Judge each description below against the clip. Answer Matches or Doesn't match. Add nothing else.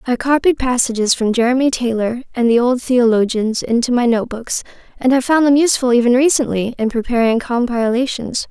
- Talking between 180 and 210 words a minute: Doesn't match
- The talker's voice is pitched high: Matches